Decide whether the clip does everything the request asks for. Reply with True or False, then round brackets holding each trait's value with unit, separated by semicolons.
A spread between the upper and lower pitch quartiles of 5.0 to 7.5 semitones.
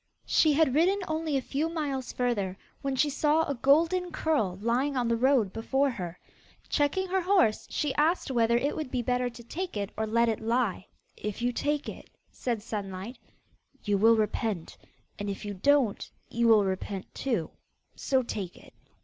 True (5.4 semitones)